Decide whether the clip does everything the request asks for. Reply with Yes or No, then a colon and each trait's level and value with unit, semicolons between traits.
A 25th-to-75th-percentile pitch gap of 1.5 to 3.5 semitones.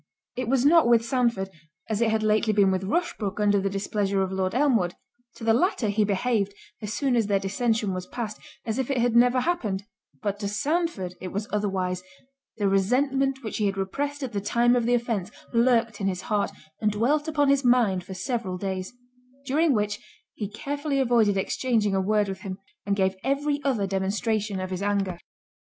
No: average, 4.2 semitones